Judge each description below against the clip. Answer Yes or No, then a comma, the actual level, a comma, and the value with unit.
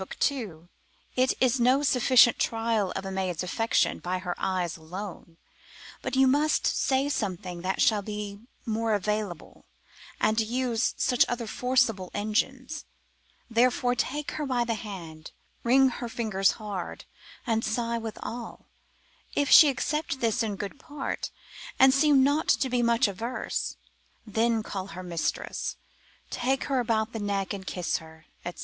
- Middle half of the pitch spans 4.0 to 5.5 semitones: Yes, average, 4.7 semitones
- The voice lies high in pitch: Yes, high, 225 Hz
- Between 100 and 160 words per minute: Yes, average, 145 wpm